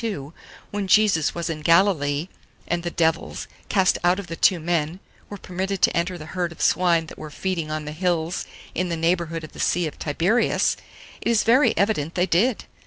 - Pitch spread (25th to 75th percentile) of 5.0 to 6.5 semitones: No, average, 2.7 semitones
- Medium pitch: Yes, medium, 175 Hz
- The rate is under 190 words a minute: No, average, 200 wpm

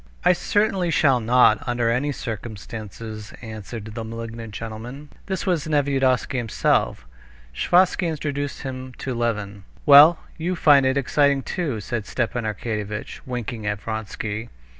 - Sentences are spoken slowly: Yes, slow, 130 wpm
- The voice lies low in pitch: Yes, low, 120 Hz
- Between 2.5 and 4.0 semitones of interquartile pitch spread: No, average, 4.5 semitones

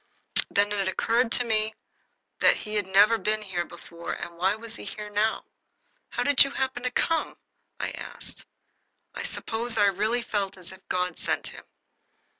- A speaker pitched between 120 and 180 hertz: No, high, 210 Hz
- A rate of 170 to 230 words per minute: Yes, average, 175 wpm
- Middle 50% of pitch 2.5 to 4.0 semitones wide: Yes, average, 3.2 semitones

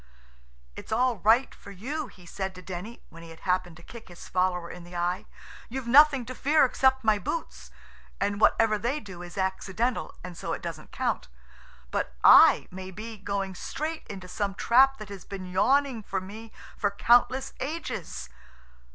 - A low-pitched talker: No, high, 205 Hz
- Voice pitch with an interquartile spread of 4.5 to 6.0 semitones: Yes, wide, 5.4 semitones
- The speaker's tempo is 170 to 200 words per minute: Yes, average, 175 wpm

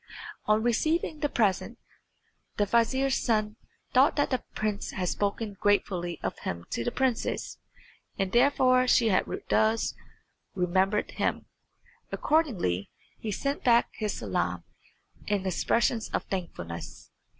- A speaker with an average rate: No, slow, 125 wpm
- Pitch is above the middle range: Yes, high, 215 Hz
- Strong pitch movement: No, average, 4.8 semitones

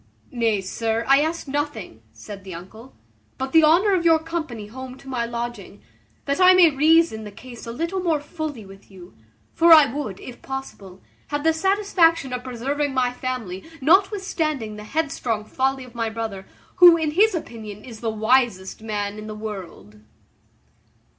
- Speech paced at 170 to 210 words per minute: Yes, average, 175 wpm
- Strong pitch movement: Yes, wide, 6.5 semitones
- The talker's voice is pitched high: Yes, very high, 255 Hz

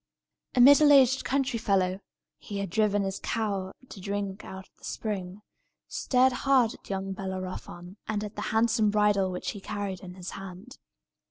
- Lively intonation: No, average, 2.8 semitones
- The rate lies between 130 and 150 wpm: No, average, 170 wpm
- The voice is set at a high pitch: Yes, high, 205 Hz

